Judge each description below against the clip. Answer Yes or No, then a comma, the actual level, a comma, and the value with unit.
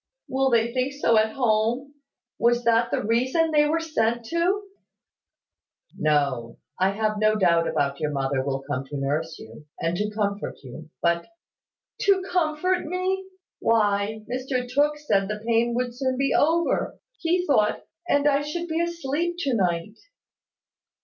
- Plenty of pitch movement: Yes, wide, 7.5 semitones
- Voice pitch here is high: Yes, high, 235 Hz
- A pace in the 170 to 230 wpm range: No, average, 155 wpm